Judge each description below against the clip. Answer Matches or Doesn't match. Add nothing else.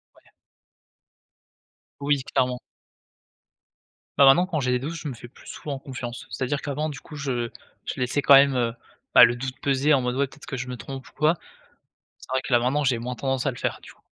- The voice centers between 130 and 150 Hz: Matches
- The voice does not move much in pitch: Matches